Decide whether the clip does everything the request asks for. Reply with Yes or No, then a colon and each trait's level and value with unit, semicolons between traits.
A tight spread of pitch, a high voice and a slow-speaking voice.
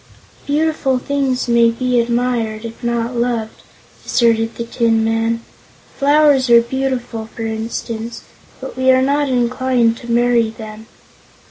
Yes: narrow, 2.2 semitones; high, 235 Hz; slow, 130 wpm